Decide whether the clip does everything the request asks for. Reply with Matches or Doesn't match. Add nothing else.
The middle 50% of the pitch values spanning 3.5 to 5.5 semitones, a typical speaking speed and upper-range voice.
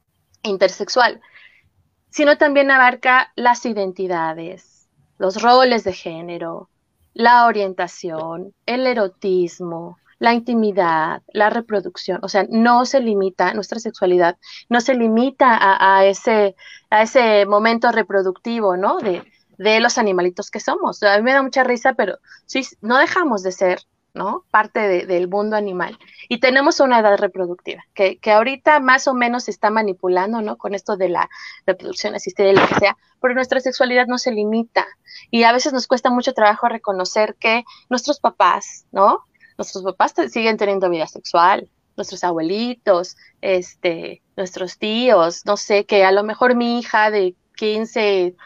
Matches